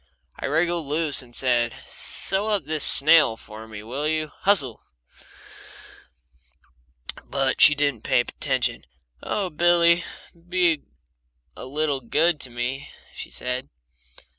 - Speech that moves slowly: Yes, slow, 125 wpm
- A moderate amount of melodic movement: Yes, average, 4.9 semitones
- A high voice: No, medium, 145 Hz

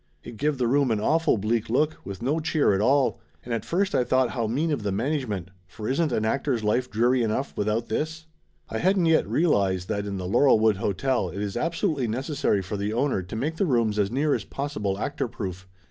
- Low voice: Yes, low, 120 Hz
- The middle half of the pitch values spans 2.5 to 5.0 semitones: No, wide, 5.6 semitones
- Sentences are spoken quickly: Yes, fast, 220 wpm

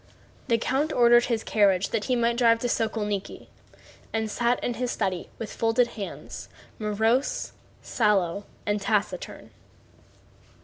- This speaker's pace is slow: Yes, slow, 130 wpm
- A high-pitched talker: Yes, high, 225 Hz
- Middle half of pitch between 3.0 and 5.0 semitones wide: No, narrow, 2.5 semitones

